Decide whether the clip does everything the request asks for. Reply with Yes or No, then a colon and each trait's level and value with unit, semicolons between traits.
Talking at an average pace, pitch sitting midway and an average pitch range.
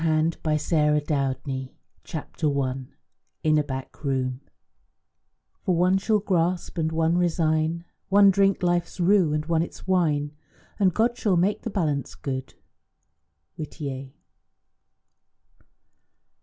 No: slow, 120 wpm; medium, 160 Hz; average, 3.6 semitones